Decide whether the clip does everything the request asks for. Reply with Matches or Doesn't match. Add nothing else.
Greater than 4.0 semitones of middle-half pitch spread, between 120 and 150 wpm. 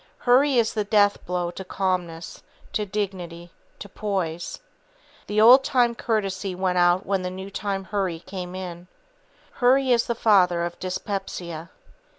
Doesn't match